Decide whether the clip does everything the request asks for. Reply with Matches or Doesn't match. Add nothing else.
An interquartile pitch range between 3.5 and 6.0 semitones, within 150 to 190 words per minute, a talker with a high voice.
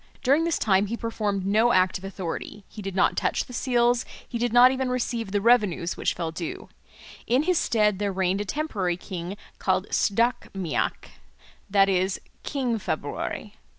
Matches